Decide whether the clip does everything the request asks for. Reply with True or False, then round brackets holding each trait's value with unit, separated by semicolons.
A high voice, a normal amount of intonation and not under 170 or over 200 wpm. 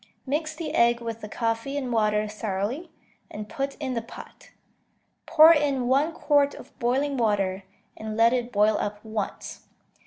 False (235 Hz; 4.7 semitones; 160 wpm)